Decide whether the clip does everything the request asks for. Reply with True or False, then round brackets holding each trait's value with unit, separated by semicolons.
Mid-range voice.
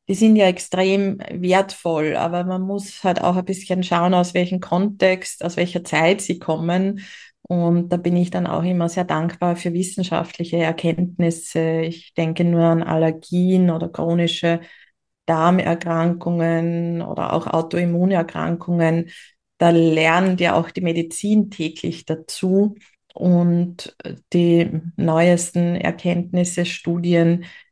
True (175 Hz)